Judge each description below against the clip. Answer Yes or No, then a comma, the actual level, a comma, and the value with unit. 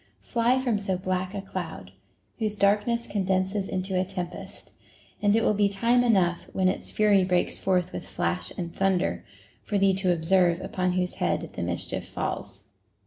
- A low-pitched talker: No, high, 190 Hz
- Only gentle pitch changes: Yes, narrow, 2.2 semitones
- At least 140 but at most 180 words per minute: Yes, average, 175 wpm